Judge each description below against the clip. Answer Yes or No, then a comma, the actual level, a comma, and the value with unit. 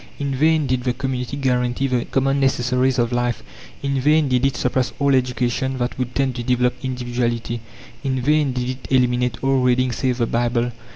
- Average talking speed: Yes, average, 185 wpm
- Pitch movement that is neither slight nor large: No, narrow, 1.5 semitones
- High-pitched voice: No, low, 125 Hz